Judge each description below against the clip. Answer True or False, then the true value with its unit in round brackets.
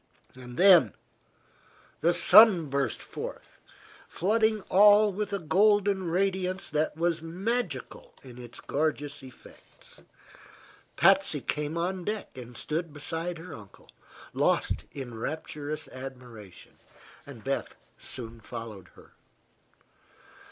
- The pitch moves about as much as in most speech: False (6.6 semitones)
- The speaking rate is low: True (100 wpm)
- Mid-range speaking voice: True (160 Hz)